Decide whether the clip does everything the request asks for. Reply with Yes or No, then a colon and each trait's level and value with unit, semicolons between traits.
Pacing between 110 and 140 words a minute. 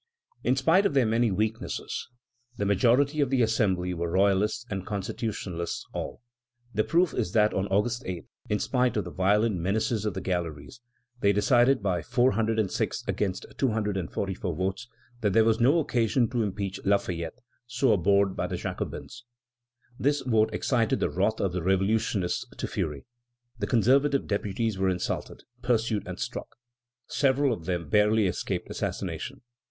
No: average, 155 wpm